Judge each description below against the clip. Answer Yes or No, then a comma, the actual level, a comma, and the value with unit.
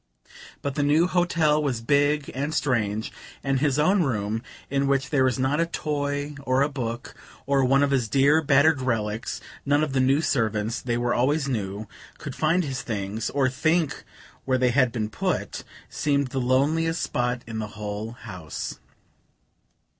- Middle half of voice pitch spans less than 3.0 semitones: No, average, 3.6 semitones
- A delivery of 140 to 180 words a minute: Yes, average, 170 wpm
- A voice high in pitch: No, low, 135 Hz